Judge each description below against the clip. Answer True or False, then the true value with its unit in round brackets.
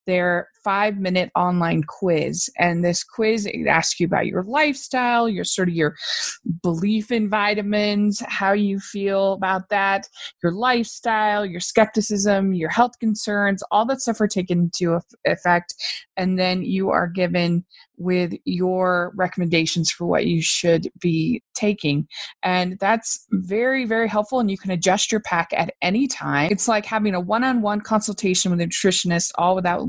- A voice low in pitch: False (195 Hz)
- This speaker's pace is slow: False (155 wpm)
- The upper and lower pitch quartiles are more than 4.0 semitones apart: False (3.4 semitones)